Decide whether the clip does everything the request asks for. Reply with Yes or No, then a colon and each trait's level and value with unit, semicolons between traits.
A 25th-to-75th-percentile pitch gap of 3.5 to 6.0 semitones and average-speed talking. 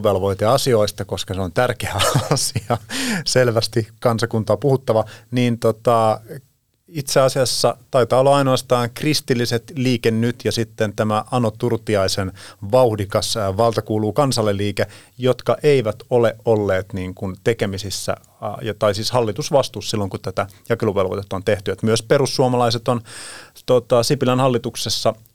No: average, 3.0 semitones; average, 120 wpm